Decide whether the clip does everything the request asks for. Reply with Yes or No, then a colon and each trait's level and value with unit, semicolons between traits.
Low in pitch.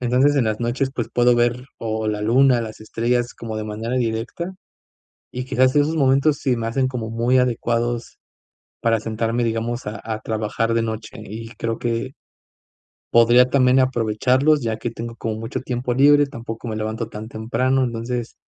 Yes: low, 120 Hz